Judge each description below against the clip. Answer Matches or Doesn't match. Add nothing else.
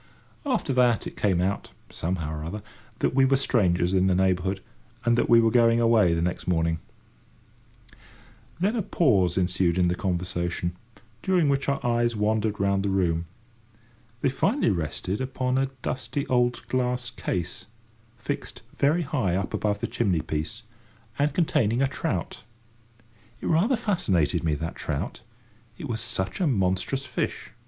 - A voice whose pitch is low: Matches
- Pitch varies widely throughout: Matches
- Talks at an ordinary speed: Matches